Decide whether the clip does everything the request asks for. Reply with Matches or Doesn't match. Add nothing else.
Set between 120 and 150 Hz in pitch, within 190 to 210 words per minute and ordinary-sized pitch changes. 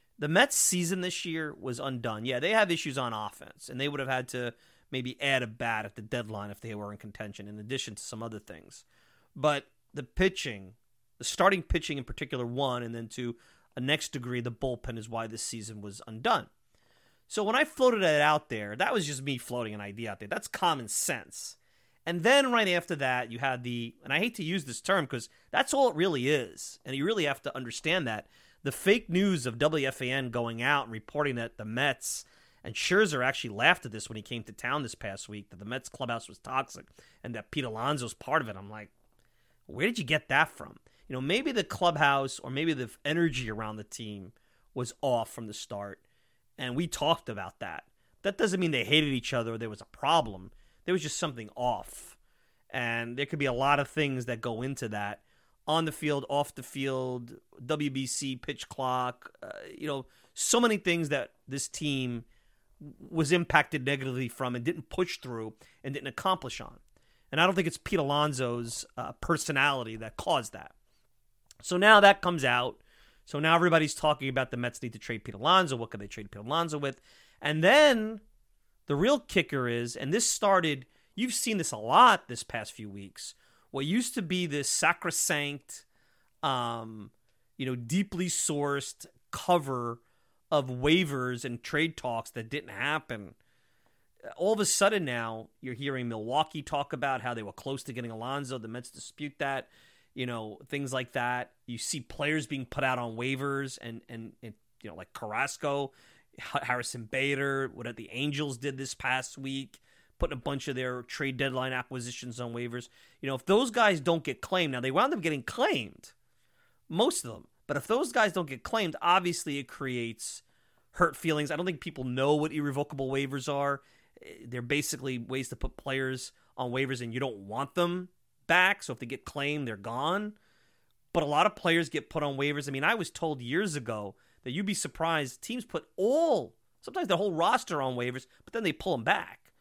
Matches